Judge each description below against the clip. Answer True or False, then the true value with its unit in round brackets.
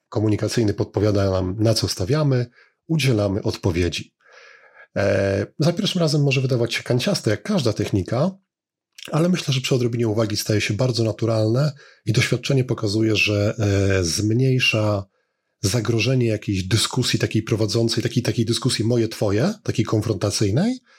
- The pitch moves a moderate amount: True (3.6 semitones)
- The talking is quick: False (130 wpm)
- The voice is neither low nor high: False (115 Hz)